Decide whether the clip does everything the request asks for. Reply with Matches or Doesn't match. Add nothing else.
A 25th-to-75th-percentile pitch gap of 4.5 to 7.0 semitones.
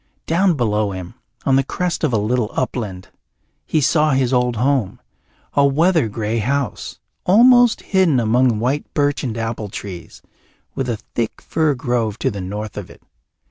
Matches